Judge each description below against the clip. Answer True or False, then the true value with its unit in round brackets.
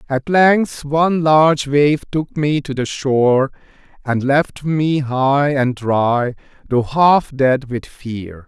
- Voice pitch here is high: False (140 Hz)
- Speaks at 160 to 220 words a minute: False (150 wpm)